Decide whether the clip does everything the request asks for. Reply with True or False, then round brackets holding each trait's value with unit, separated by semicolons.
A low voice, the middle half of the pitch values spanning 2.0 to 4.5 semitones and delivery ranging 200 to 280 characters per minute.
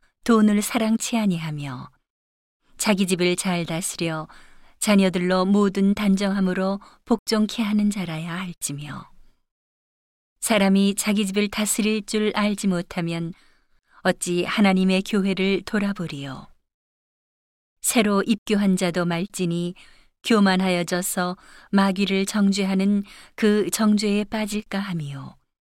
False (195 Hz; 2.9 semitones; 235 characters per minute)